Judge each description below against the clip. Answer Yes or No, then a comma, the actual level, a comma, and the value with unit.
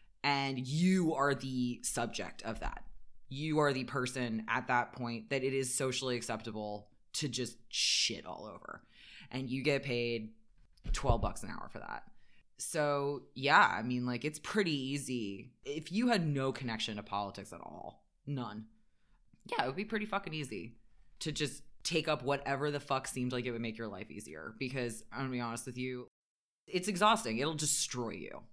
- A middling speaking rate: Yes, average, 180 wpm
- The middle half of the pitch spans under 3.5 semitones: No, average, 3.9 semitones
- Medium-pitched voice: No, low, 130 Hz